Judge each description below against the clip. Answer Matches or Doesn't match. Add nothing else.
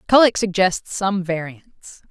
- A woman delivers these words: Matches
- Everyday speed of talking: Doesn't match